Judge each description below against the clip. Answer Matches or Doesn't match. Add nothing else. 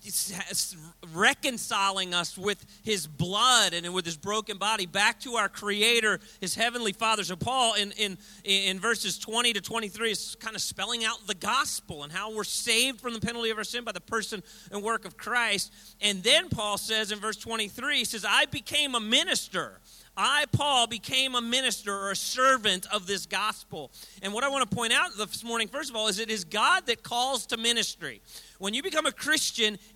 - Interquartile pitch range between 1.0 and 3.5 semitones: Matches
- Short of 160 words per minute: Doesn't match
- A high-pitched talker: Matches